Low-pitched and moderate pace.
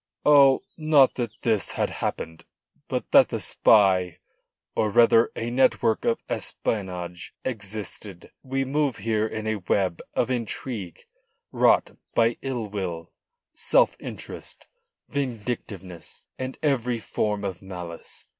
No: low, 110 Hz; slow, 120 wpm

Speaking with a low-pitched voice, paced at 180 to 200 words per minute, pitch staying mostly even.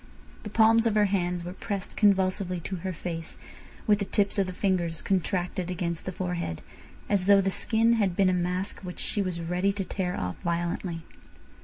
No: medium, 185 Hz; average, 190 wpm; narrow, 2.2 semitones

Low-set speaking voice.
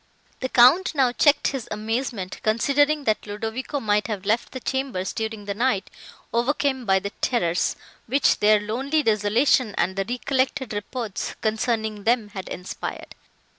No: high, 225 Hz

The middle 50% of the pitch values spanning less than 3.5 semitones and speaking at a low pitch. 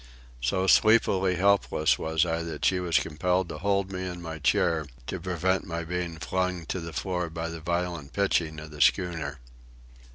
Yes: narrow, 2.5 semitones; very low, 85 Hz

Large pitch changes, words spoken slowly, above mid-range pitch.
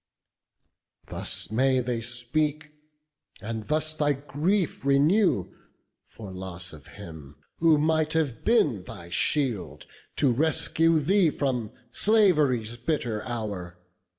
No: wide, 6.1 semitones; slow, 110 wpm; low, 135 Hz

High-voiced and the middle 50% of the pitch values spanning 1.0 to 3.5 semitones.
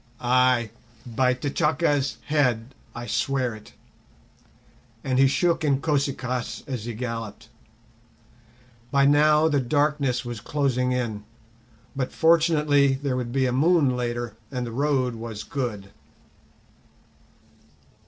No: low, 130 Hz; average, 3.0 semitones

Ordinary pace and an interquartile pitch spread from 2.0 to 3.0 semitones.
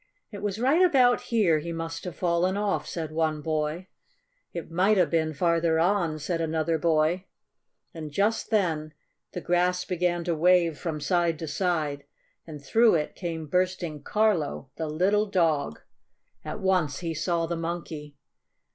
Yes: average, 155 wpm; average, 2.7 semitones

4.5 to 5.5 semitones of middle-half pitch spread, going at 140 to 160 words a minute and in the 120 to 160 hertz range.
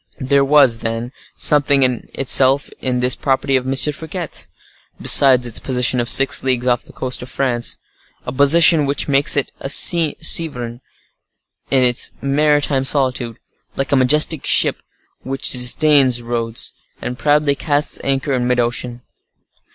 No: narrow, 2.5 semitones; average, 145 wpm; low, 135 Hz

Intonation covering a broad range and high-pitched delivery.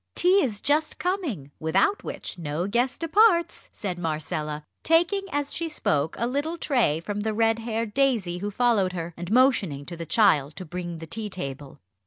Yes: wide, 8.8 semitones; high, 205 Hz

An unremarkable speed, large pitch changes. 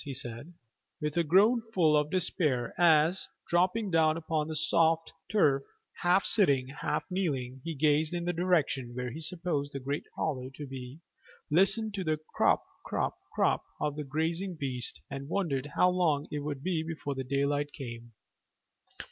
No: average, 165 wpm; average, 4.1 semitones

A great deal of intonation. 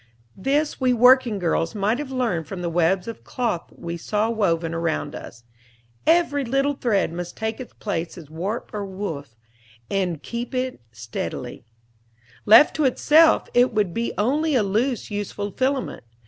Yes: wide, 6.5 semitones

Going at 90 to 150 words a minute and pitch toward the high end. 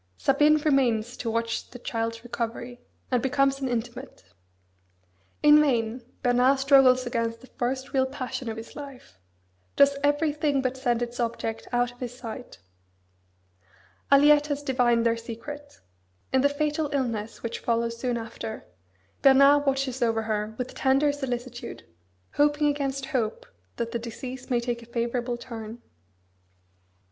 Yes: average, 140 wpm; very high, 250 Hz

